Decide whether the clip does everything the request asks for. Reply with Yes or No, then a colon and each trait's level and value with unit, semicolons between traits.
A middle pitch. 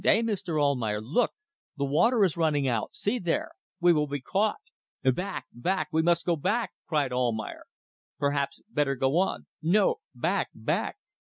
Yes: medium, 155 Hz